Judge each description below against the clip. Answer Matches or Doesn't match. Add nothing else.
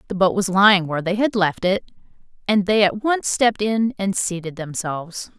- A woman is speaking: Matches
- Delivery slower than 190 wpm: Doesn't match